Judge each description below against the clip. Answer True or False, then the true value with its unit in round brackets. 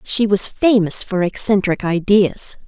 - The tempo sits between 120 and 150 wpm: True (135 wpm)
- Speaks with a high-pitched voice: True (200 Hz)